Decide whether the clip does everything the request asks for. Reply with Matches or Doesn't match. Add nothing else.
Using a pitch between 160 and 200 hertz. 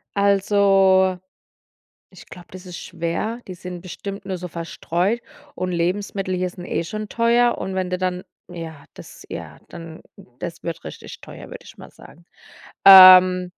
Matches